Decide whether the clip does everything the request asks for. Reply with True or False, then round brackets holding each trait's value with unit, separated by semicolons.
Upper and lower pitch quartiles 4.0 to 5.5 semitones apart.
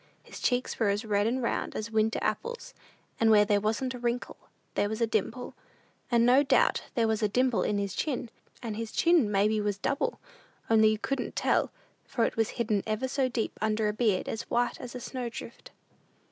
False (2.7 semitones)